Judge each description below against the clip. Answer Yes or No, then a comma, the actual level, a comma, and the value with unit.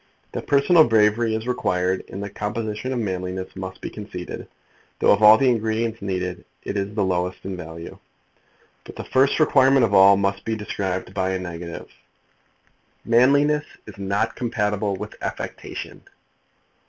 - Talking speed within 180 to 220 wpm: No, average, 155 wpm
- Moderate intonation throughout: Yes, average, 3.6 semitones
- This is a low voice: Yes, low, 105 Hz